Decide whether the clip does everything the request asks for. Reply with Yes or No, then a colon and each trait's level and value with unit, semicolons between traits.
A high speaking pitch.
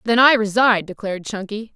Yes: high, 215 Hz